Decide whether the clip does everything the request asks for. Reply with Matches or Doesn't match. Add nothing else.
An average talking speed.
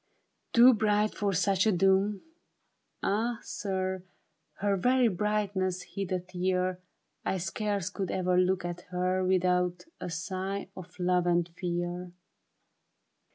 Doesn't match